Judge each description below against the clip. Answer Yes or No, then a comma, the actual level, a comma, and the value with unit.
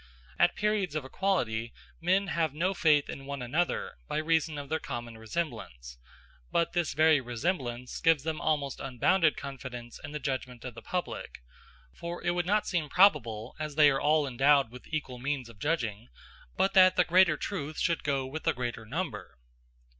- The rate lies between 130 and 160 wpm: No, average, 175 wpm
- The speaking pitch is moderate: Yes, medium, 145 Hz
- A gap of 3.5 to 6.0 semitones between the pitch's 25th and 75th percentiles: Yes, average, 5.2 semitones